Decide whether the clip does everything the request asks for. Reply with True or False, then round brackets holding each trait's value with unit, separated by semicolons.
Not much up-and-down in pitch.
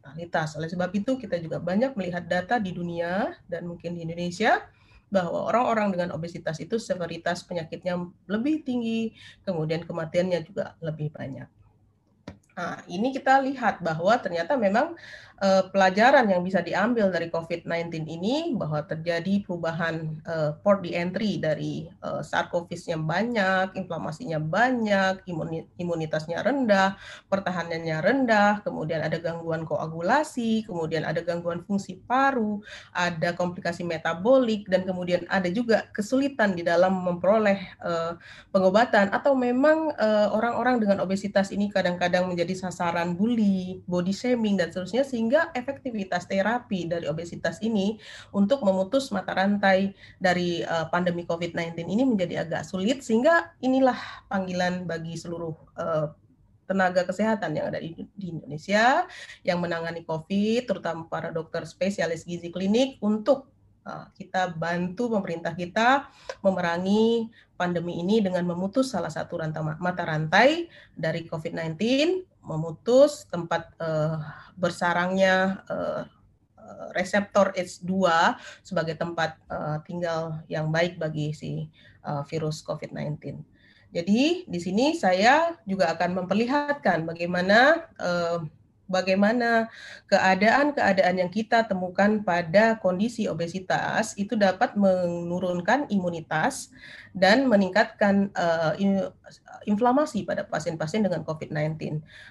False (4.2 semitones)